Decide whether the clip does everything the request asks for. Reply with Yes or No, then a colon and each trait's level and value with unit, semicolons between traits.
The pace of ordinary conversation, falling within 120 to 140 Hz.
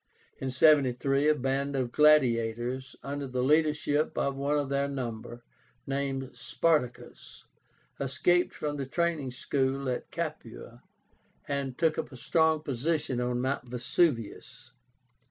No: slow, 125 wpm; low, 135 Hz